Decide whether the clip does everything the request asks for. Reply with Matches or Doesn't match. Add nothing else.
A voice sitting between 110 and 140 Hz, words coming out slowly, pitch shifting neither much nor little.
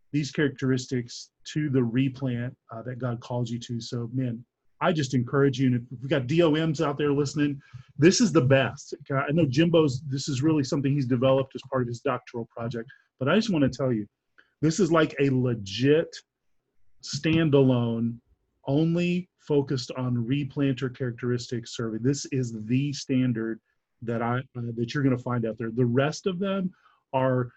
Doesn't match